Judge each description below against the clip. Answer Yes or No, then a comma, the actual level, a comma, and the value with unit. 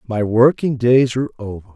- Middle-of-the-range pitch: No, low, 120 Hz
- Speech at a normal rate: Yes, average, 170 wpm